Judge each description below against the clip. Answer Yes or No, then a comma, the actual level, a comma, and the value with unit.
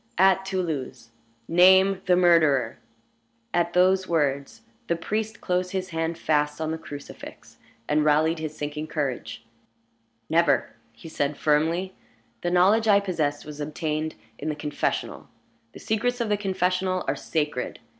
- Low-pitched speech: No, medium, 165 Hz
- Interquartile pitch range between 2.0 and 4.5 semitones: Yes, average, 3.8 semitones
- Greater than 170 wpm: No, average, 140 wpm